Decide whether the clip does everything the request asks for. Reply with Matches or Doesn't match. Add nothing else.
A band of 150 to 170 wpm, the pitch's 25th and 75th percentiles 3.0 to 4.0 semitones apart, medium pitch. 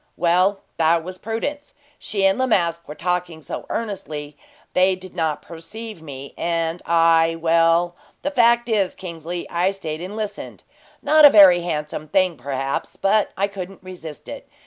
Matches